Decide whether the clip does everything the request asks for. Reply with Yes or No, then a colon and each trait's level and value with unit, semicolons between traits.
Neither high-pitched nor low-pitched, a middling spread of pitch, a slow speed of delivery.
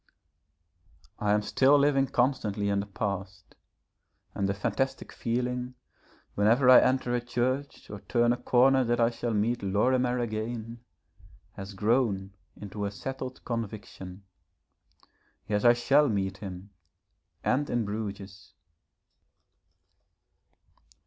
No: low, 115 Hz; average, 3.7 semitones; slow, 120 wpm